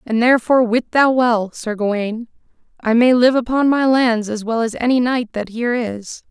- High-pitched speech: Yes, high, 235 Hz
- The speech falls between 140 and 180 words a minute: No, average, 200 wpm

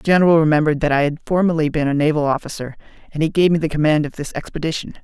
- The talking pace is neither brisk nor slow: No, fast, 240 wpm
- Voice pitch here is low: No, medium, 155 Hz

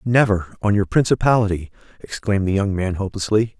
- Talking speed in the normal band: Yes, average, 150 wpm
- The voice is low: Yes, low, 100 Hz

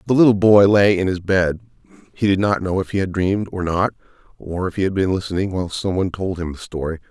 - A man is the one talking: Yes, male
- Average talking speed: No, fast, 245 wpm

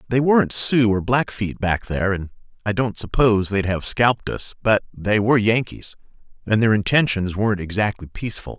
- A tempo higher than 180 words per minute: No, average, 175 wpm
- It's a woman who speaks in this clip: No, male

